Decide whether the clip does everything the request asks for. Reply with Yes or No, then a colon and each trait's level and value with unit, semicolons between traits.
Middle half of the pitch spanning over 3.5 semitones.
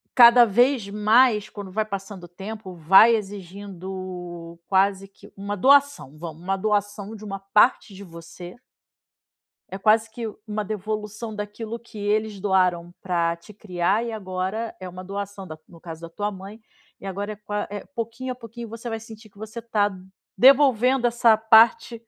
No: average, 3.0 semitones